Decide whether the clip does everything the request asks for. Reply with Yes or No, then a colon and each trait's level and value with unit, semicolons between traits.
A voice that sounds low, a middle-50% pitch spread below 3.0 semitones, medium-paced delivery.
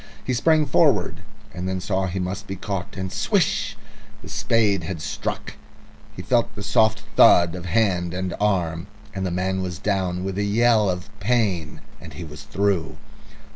Yes: very low, 95 Hz; narrow, 2.5 semitones; average, 175 wpm